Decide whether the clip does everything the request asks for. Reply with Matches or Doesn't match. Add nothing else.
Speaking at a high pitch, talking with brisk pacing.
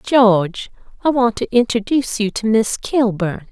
Doesn't match